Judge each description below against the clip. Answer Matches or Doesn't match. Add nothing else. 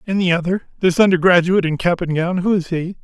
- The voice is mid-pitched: Matches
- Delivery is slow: Doesn't match